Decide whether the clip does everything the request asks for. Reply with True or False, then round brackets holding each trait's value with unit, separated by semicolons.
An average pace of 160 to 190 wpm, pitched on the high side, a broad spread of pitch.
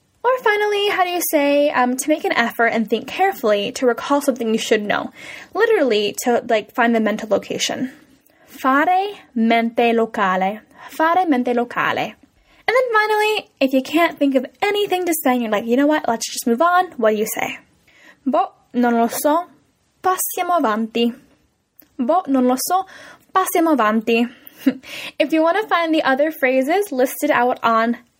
True (170 wpm; 275 Hz; 6.6 semitones)